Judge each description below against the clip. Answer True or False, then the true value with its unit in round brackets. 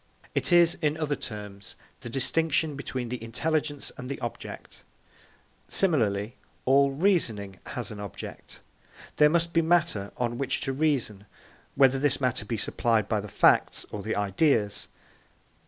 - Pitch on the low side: True (130 Hz)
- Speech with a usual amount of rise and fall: False (6.2 semitones)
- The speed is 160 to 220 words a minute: False (145 wpm)